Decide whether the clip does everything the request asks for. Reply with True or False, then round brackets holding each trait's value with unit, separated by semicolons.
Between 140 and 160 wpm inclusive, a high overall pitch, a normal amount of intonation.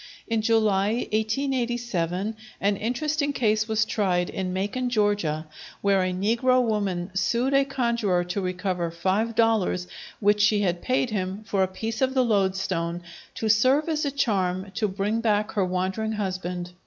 True (155 wpm; 210 Hz; 3.6 semitones)